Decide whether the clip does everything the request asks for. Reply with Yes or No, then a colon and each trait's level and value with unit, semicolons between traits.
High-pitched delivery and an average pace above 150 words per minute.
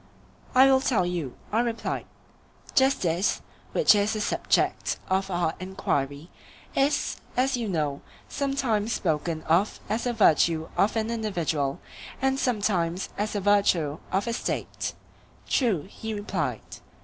No: high, 205 Hz; slow, 135 wpm